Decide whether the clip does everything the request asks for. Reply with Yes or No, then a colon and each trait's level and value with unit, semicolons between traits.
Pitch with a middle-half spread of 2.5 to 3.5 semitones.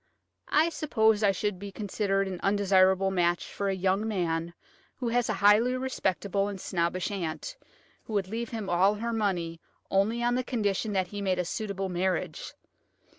Yes: average, 2.8 semitones